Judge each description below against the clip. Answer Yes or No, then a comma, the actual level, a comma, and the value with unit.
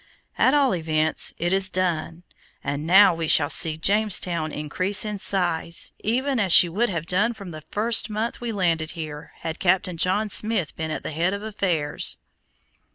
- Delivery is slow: No, average, 175 wpm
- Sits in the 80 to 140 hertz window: No, medium, 180 Hz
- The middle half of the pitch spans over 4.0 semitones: Yes, average, 4.5 semitones